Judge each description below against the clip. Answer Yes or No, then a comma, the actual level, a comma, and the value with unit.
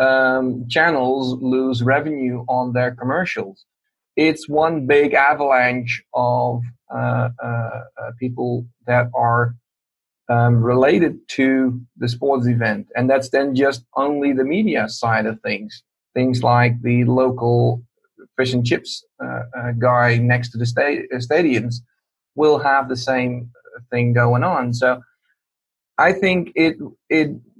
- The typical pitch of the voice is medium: No, low, 125 Hz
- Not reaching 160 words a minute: Yes, slow, 135 wpm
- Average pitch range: No, narrow, 1.9 semitones